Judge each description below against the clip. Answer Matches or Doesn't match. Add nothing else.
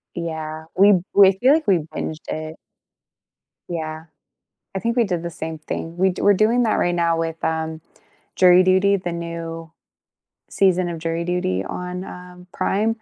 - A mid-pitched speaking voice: Matches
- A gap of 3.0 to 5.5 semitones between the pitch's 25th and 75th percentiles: Doesn't match